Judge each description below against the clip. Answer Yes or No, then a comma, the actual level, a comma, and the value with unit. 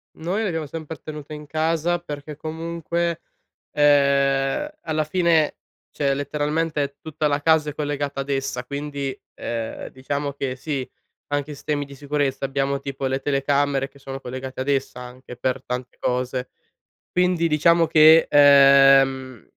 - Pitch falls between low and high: Yes, medium, 145 Hz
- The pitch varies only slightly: Yes, narrow, 2.2 semitones